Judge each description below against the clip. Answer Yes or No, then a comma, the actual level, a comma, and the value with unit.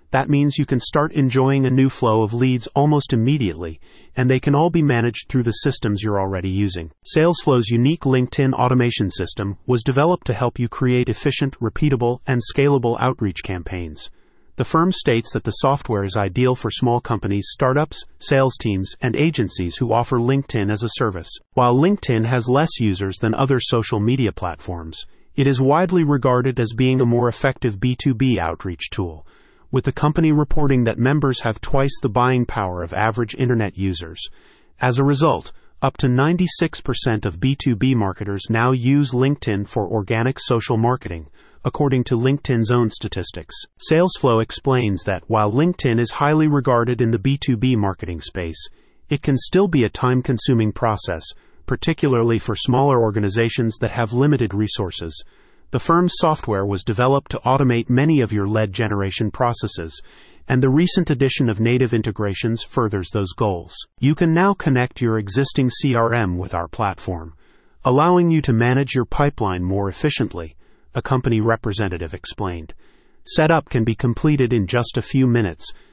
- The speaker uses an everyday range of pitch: Yes, average, 4.2 semitones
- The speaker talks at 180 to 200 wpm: No, average, 160 wpm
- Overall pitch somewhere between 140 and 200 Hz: No, low, 120 Hz